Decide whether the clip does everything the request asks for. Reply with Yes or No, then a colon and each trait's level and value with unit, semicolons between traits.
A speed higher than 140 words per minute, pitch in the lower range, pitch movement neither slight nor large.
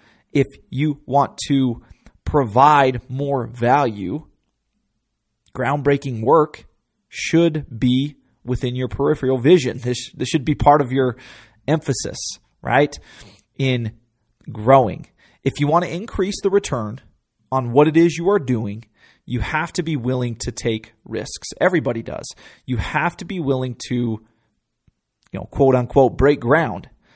No: slow, 135 wpm; low, 130 Hz; average, 3.6 semitones